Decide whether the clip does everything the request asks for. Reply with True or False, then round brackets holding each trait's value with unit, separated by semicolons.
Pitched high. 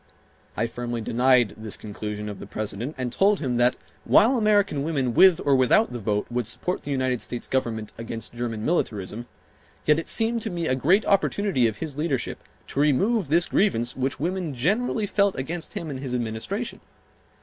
False (130 Hz)